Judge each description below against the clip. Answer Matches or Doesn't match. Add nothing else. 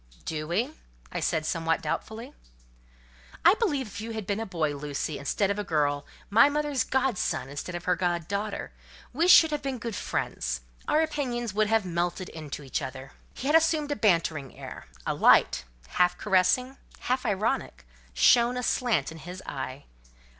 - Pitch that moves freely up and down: Matches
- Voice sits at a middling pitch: Doesn't match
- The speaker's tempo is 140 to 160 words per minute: Doesn't match